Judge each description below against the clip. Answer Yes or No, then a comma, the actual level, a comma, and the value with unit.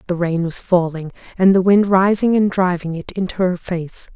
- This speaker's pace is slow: No, average, 200 wpm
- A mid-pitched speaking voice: Yes, medium, 180 Hz